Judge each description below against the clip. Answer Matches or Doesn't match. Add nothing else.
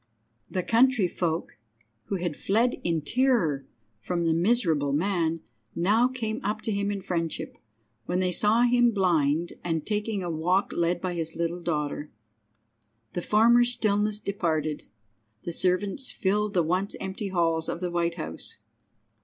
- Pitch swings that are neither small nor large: Matches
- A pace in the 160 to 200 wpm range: Doesn't match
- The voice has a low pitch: Doesn't match